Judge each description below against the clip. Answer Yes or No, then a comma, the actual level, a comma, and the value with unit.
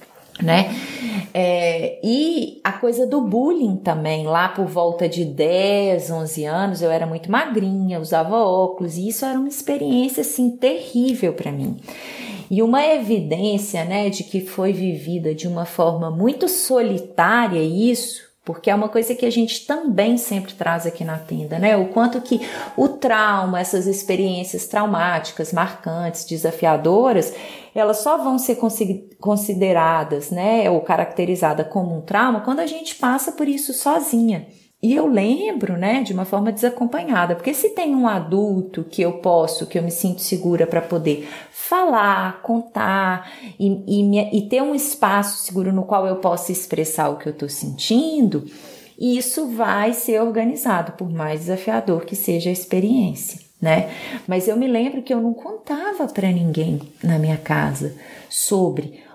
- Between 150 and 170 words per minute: Yes, average, 155 wpm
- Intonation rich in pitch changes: Yes, wide, 5.8 semitones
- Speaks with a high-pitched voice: Yes, high, 200 Hz